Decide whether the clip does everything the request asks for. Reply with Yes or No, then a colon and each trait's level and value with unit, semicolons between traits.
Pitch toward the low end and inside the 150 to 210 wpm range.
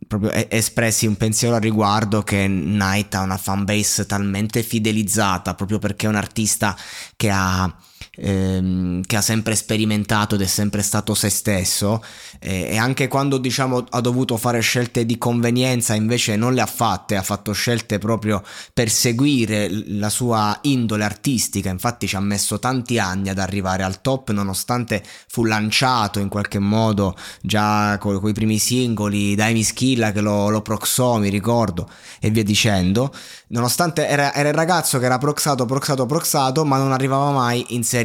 Yes: low, 110 Hz; average, 165 wpm